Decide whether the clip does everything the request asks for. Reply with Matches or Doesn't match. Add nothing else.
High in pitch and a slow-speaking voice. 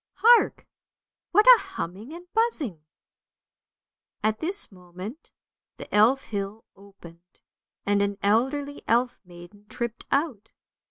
Matches